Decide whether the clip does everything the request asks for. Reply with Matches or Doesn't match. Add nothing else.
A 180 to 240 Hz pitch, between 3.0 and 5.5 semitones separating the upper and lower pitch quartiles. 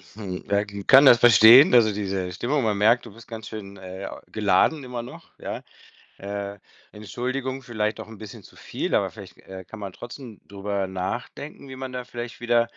Doesn't match